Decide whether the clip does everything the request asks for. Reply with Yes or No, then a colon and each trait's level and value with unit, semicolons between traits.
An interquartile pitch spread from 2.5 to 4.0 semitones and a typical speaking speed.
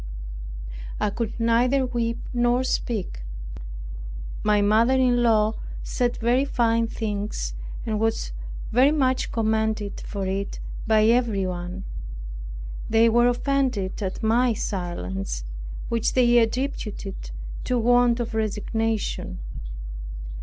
No: average, 2.8 semitones; slow, 105 wpm